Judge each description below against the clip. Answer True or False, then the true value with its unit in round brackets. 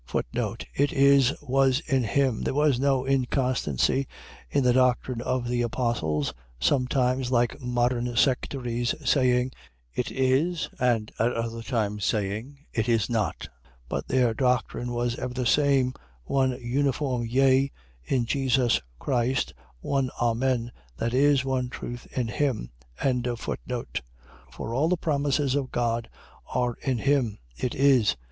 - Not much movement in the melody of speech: True (2.2 semitones)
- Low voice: True (125 Hz)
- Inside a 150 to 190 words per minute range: False (135 wpm)